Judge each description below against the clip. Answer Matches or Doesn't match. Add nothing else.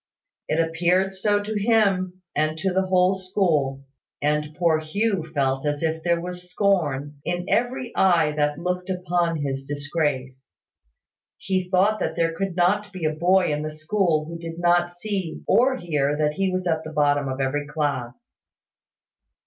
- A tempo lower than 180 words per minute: Matches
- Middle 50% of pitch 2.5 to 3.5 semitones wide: Doesn't match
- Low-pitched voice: Doesn't match